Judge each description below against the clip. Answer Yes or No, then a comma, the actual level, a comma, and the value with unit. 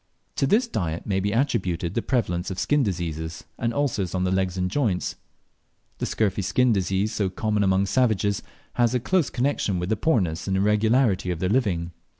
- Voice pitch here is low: Yes, low, 100 Hz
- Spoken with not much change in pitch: No, average, 4.5 semitones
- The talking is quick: No, average, 185 wpm